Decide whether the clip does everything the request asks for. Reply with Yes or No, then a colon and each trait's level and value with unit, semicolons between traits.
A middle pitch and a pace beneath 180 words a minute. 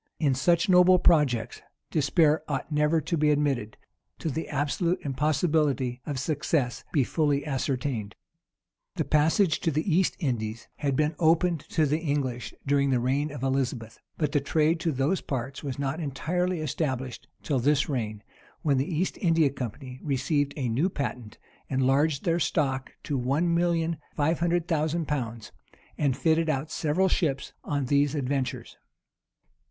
Yes: medium, 145 Hz; average, 155 wpm